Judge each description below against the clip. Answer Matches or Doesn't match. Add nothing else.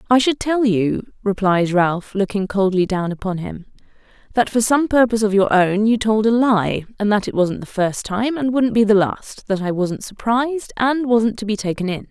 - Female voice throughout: Matches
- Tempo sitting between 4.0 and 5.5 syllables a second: Matches